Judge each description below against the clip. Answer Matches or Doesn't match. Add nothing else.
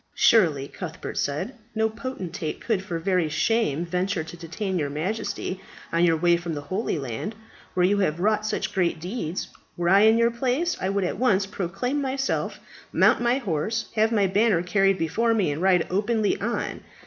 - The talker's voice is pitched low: Doesn't match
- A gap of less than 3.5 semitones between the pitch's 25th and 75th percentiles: Doesn't match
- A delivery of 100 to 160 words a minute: Doesn't match